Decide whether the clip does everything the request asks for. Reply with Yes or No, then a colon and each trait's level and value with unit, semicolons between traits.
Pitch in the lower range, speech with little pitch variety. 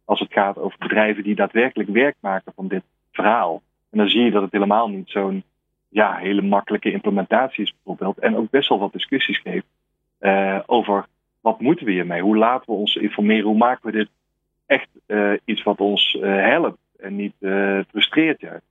Yes: low, 105 Hz; narrow, 1.8 semitones